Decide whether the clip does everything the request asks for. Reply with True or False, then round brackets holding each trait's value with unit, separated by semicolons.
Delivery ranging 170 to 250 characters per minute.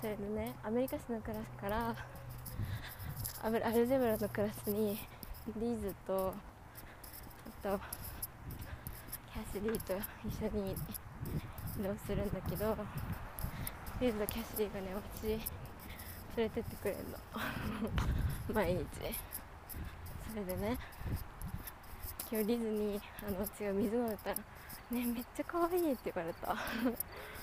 True (230 characters per minute)